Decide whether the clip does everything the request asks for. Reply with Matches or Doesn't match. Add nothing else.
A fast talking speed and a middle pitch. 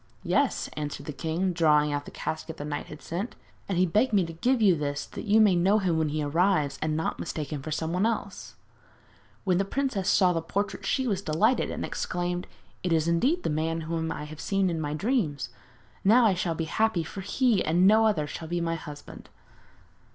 Matches